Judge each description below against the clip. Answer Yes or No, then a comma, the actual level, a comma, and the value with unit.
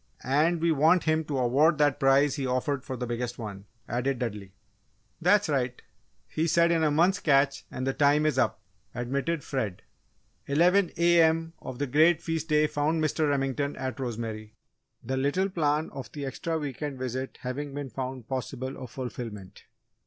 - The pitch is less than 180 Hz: Yes, medium, 140 Hz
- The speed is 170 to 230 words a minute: Yes, average, 175 wpm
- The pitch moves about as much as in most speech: Yes, average, 3.7 semitones